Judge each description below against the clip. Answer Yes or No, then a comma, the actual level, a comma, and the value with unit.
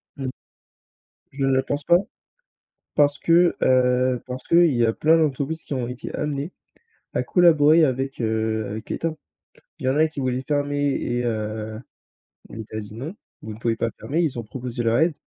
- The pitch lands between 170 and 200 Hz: No, low, 130 Hz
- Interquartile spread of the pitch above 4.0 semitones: Yes, average, 4.4 semitones